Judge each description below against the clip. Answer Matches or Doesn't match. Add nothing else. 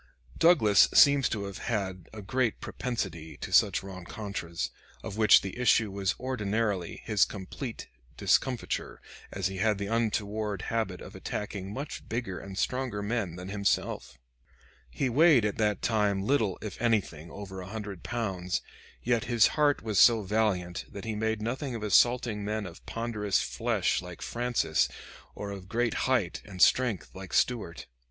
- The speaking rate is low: Doesn't match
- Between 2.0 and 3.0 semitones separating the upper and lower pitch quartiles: Doesn't match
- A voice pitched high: Doesn't match